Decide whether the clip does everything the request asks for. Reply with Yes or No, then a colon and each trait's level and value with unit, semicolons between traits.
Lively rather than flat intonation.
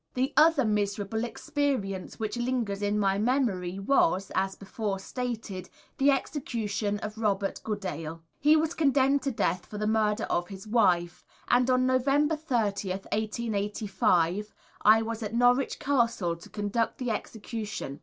No: average, 4.2 semitones